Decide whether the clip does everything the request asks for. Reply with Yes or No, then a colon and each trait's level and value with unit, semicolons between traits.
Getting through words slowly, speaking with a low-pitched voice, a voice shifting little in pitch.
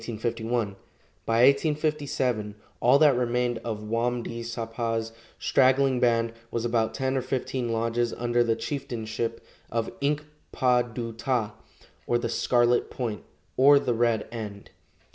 Yes: slow, 130 wpm; low, 120 Hz; narrow, 2.0 semitones